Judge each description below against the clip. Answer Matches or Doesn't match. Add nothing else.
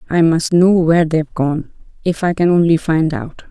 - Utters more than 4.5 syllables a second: Matches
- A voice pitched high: Doesn't match